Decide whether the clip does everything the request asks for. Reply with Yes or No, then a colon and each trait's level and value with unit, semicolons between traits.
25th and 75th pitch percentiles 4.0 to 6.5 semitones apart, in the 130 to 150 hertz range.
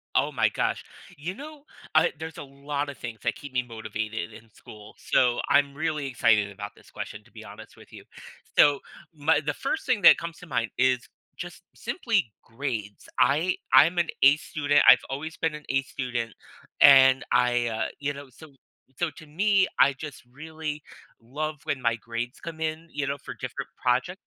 Yes: average, 4.3 semitones; medium, 140 Hz